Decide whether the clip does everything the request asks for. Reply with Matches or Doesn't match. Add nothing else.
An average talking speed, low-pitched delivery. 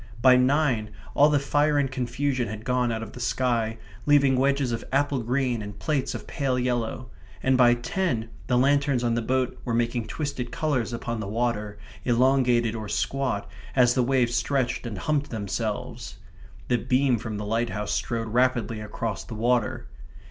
Matches